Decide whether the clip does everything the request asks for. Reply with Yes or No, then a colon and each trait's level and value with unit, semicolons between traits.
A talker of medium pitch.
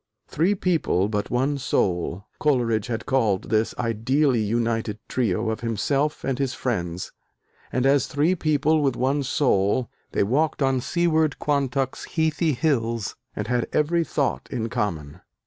No: low, 130 Hz